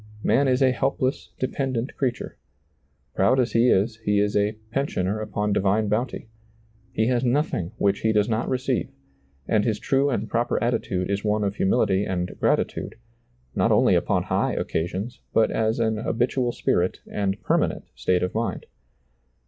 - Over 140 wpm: Yes, average, 165 wpm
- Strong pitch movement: No, average, 3.5 semitones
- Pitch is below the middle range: Yes, low, 110 Hz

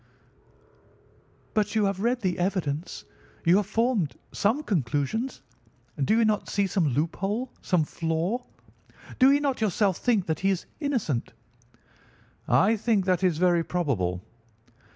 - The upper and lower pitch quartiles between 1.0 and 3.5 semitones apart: No, average, 5.1 semitones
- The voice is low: No, high, 195 Hz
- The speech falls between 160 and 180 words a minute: No, average, 140 wpm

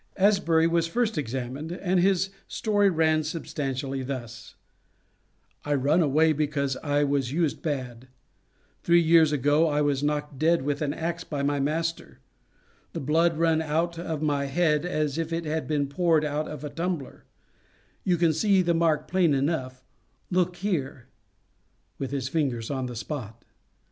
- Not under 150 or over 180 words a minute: Yes, average, 160 wpm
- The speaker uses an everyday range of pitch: Yes, average, 3.1 semitones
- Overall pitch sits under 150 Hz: No, medium, 155 Hz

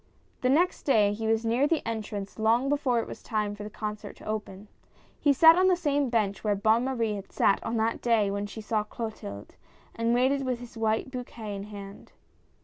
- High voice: Yes, high, 225 Hz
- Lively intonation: No, average, 3.3 semitones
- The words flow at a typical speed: No, fast, 215 wpm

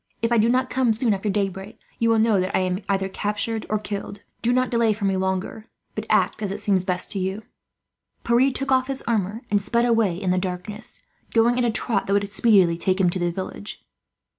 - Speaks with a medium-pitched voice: No, high, 210 Hz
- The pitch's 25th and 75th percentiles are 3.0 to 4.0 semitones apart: Yes, average, 3.3 semitones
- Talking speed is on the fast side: Yes, fast, 225 wpm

